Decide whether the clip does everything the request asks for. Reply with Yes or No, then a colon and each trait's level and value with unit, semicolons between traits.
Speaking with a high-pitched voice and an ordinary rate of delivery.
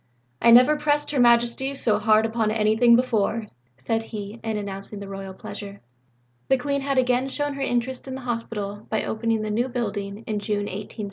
Yes: high, 225 Hz; average, 190 wpm